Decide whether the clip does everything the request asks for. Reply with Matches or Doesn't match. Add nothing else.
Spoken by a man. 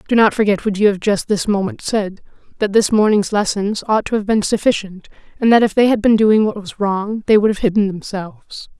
Doesn't match